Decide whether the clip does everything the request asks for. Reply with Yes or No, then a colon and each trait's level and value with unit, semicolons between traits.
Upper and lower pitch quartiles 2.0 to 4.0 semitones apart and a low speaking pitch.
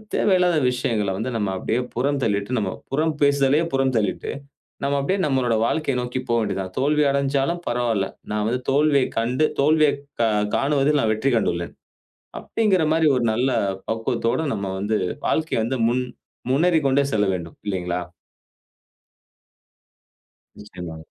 No: average, 4.9 semitones; low, 130 Hz